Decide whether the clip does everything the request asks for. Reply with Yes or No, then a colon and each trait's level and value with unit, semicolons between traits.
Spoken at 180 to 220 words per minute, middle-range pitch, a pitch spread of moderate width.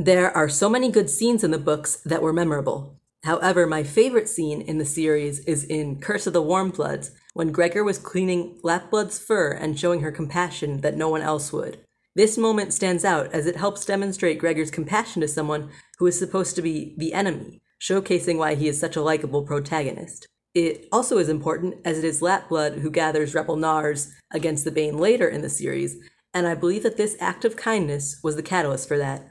Yes: fast, 205 wpm; medium, 165 Hz; average, 3.3 semitones